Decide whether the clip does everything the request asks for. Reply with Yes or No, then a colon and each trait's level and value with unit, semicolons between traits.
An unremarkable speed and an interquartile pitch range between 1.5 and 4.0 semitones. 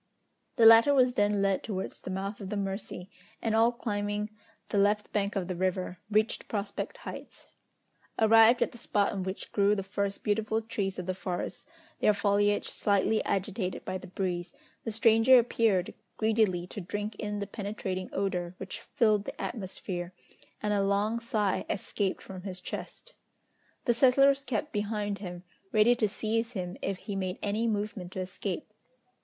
Yes: average, 170 wpm; narrow, 2.6 semitones